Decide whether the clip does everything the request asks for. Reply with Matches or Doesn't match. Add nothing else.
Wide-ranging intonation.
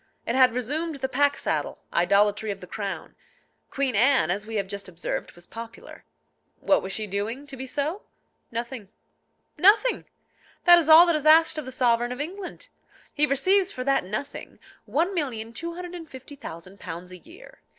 Matches